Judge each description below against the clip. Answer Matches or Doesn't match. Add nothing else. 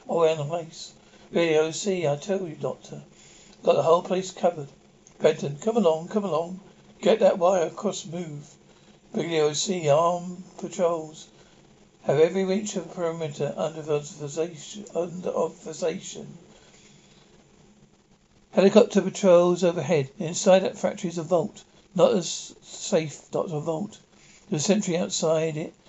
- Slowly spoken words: Matches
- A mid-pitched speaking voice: Matches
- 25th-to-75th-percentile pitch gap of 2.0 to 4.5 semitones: Matches